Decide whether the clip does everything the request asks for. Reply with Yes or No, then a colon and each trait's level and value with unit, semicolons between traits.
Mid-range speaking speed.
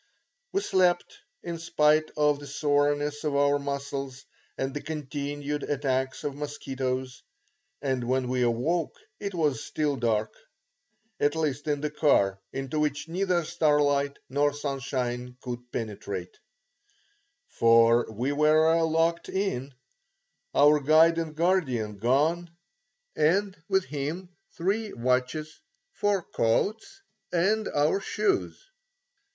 No: slow, 115 wpm